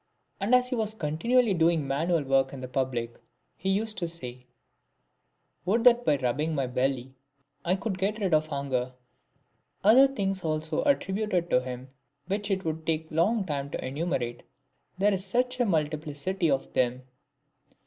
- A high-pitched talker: No, medium, 165 Hz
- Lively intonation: Yes, wide, 6.7 semitones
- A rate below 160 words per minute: No, average, 170 wpm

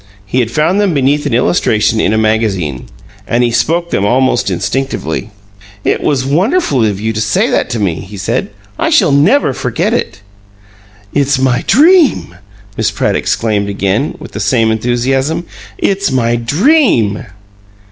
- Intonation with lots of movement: Yes, wide, 6.0 semitones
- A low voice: Yes, low, 125 Hz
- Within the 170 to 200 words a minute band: No, average, 155 wpm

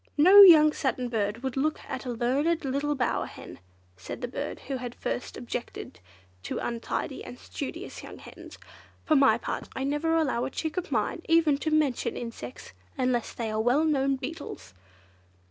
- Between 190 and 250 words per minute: No, average, 175 wpm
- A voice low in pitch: No, very high, 270 Hz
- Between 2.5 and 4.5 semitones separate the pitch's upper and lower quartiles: Yes, average, 4.1 semitones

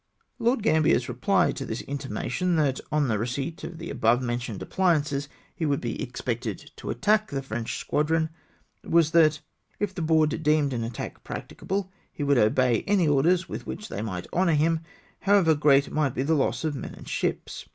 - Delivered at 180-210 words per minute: Yes, average, 190 wpm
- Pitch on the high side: No, medium, 150 Hz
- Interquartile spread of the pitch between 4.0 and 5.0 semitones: Yes, average, 4.6 semitones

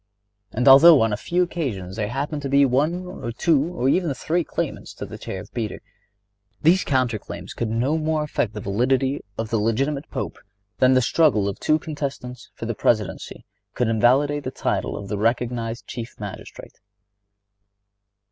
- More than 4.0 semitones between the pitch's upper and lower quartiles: Yes, average, 4.7 semitones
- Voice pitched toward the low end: Yes, low, 125 Hz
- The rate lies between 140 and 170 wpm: Yes, average, 165 wpm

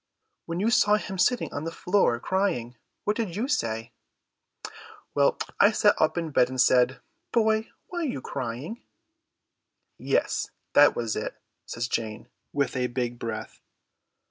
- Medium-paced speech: Yes, average, 150 wpm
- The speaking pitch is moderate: Yes, medium, 155 Hz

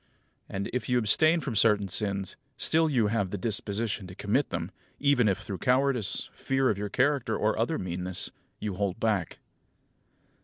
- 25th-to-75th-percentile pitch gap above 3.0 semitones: Yes, average, 4.3 semitones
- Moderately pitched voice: No, low, 110 Hz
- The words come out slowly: No, average, 165 wpm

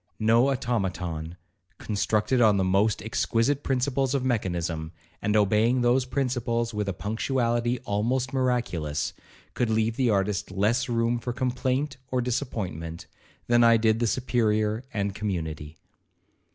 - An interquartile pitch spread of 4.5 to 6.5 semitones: No, average, 3.7 semitones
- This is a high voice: No, low, 115 Hz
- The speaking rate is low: Yes, slow, 130 wpm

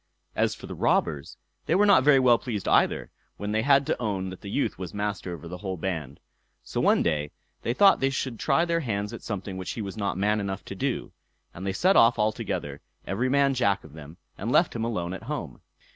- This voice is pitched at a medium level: No, low, 105 Hz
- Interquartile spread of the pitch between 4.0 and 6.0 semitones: Yes, average, 5.2 semitones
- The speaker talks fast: Yes, fast, 235 wpm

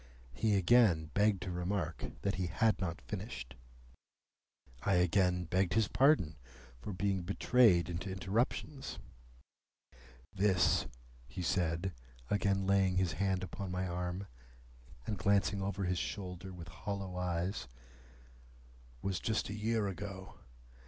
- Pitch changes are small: Yes, narrow, 2.2 semitones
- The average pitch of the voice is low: Yes, very low, 95 Hz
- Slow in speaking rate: Yes, slow, 125 wpm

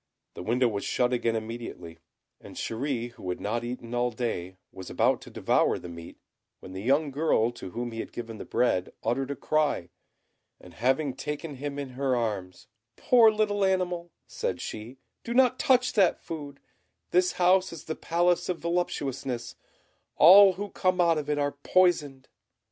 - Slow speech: No, average, 175 wpm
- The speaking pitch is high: No, low, 135 Hz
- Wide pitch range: Yes, wide, 7.0 semitones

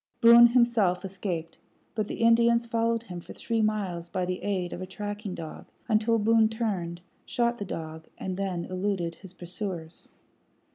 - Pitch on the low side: No, high, 200 Hz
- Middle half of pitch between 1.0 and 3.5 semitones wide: No, average, 4.3 semitones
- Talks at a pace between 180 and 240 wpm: No, average, 160 wpm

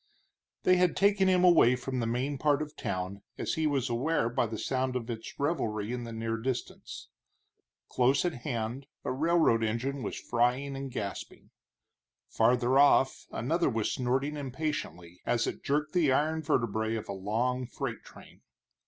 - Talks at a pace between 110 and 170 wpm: Yes, average, 165 wpm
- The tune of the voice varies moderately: Yes, average, 4.3 semitones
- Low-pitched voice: Yes, low, 125 Hz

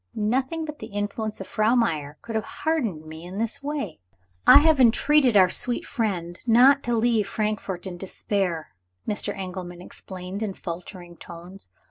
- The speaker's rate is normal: Yes, average, 160 wpm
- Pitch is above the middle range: Yes, high, 205 Hz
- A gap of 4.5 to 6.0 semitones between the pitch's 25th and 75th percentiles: Yes, average, 4.9 semitones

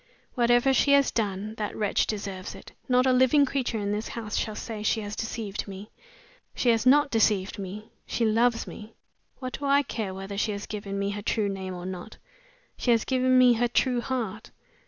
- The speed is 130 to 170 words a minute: No, average, 200 wpm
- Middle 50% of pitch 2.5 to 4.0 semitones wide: Yes, average, 3.6 semitones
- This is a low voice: No, high, 220 Hz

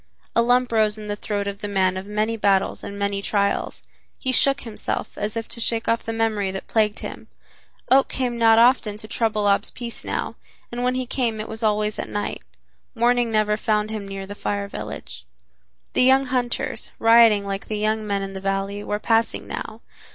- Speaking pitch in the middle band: No, high, 215 Hz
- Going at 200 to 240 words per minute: Yes, fast, 205 wpm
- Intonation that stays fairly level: Yes, narrow, 2.3 semitones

